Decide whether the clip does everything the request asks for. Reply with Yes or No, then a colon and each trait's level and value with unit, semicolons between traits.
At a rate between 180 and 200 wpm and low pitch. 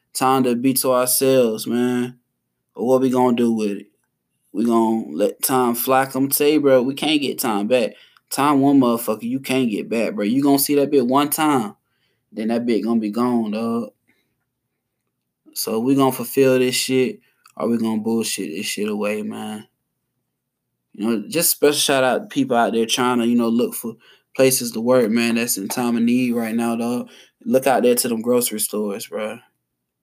Yes: average, 195 wpm; low, 125 Hz